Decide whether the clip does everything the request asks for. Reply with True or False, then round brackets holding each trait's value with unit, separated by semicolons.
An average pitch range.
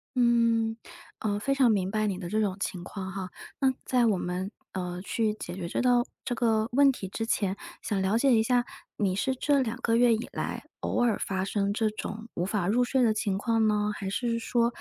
True (3.4 semitones)